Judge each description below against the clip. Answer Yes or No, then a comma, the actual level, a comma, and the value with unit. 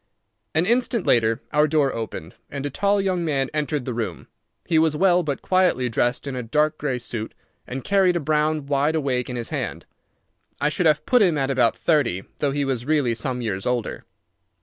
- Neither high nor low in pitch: Yes, medium, 145 Hz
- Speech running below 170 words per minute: No, average, 200 wpm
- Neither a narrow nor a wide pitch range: Yes, average, 4.2 semitones